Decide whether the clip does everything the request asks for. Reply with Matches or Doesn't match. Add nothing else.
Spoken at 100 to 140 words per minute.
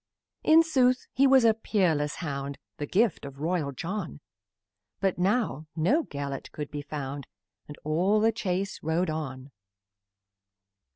Matches